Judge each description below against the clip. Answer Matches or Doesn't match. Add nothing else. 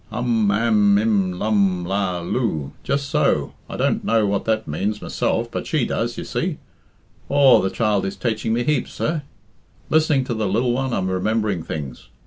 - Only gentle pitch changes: Doesn't match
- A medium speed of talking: Matches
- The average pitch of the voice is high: Doesn't match